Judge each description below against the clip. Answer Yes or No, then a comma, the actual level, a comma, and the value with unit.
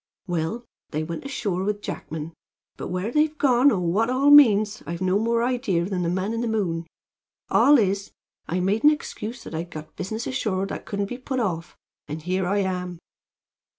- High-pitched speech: Yes, high, 200 Hz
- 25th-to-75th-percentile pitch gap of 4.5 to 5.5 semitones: Yes, average, 5.0 semitones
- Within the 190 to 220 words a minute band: Yes, average, 195 wpm